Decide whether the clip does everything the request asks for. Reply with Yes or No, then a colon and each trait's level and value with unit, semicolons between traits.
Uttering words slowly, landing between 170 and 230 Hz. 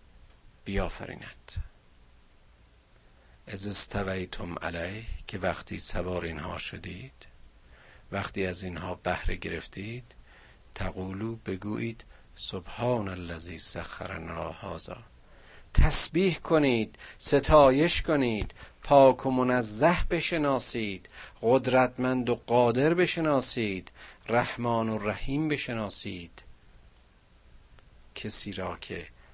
No: slow, 80 wpm; low, 100 Hz